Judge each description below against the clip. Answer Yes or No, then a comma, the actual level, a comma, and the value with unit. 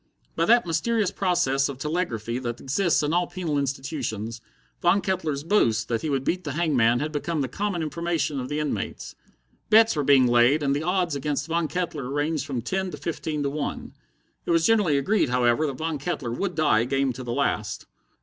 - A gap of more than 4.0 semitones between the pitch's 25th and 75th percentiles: Yes, average, 4.5 semitones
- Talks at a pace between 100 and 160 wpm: No, average, 200 wpm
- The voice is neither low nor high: Yes, medium, 150 Hz